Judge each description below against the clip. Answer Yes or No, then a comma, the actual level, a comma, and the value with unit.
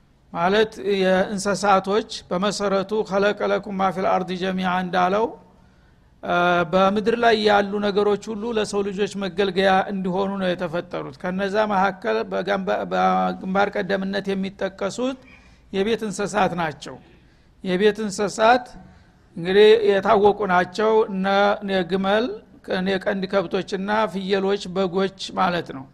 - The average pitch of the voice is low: No, high, 195 Hz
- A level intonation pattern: Yes, narrow, 1.8 semitones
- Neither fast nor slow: Yes, average, 90 wpm